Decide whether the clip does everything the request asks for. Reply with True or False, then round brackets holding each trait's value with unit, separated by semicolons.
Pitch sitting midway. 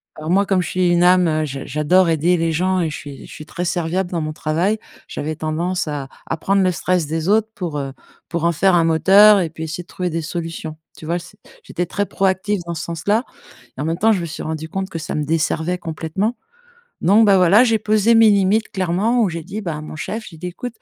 True (175 Hz)